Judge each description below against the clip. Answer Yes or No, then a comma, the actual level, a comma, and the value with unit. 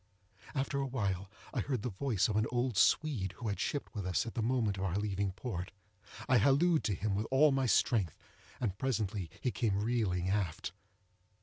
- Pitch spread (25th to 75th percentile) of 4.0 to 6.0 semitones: Yes, average, 4.9 semitones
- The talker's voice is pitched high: No, low, 110 Hz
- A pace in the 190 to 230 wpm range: Yes, average, 195 wpm